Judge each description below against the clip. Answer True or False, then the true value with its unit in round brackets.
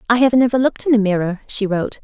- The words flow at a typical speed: False (265 wpm)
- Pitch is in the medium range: False (225 Hz)